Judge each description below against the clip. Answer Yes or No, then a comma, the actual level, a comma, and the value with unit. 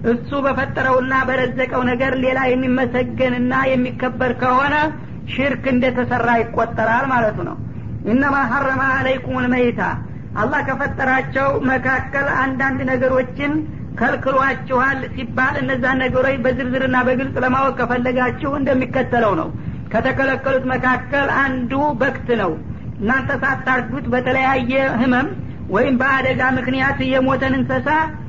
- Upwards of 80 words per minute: Yes, average, 100 wpm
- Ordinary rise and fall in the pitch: No, narrow, 0.9 semitones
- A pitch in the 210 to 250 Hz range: No, very high, 260 Hz